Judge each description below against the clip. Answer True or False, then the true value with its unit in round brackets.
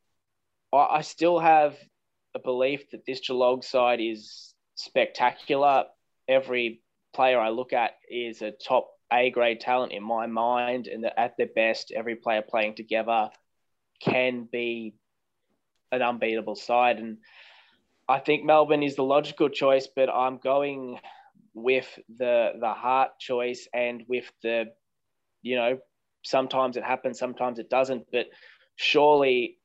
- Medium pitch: False (125 Hz)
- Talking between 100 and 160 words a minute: True (140 wpm)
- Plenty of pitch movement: False (2.5 semitones)